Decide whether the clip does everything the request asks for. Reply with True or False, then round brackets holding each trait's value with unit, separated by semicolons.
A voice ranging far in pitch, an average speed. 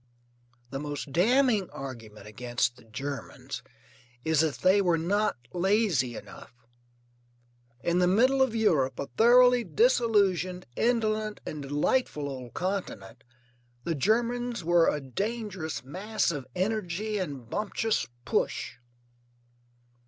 False (7.4 semitones; 115 wpm)